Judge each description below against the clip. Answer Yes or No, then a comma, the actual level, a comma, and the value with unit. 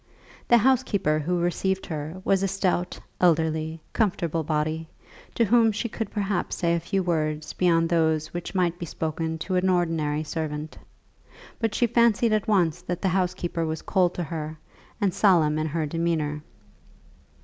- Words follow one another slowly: No, average, 160 wpm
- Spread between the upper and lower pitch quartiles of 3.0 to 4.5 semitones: Yes, average, 3.3 semitones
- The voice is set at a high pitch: No, medium, 170 Hz